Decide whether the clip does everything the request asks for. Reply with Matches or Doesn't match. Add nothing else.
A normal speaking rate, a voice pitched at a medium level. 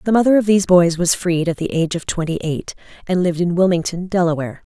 Doesn't match